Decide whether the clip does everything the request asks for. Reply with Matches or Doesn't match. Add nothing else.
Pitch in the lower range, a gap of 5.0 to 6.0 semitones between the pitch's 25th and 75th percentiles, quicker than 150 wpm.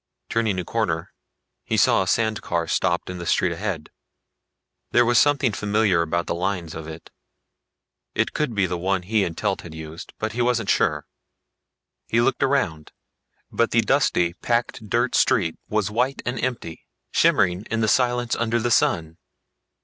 Matches